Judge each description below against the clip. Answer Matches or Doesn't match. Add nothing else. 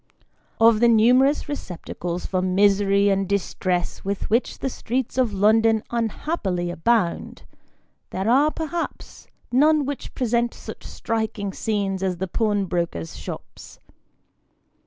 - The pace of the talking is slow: Matches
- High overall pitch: Matches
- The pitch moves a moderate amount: Matches